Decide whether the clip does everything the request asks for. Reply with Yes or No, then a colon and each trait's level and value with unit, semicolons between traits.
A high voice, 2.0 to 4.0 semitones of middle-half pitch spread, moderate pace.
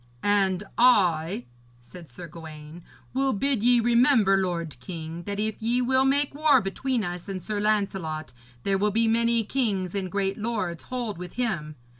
No: high, 200 Hz; average, 5.1 semitones; average, 165 wpm